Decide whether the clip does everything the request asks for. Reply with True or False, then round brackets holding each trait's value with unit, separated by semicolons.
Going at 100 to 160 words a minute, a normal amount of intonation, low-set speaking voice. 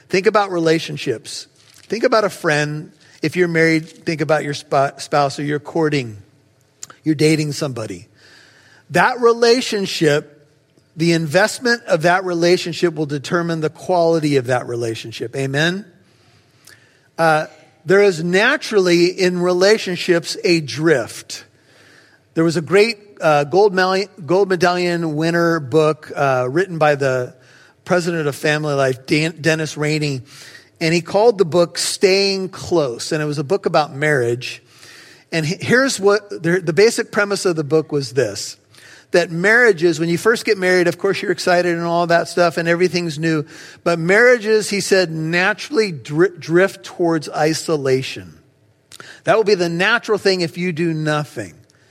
False (150 wpm; 3.6 semitones; 165 Hz)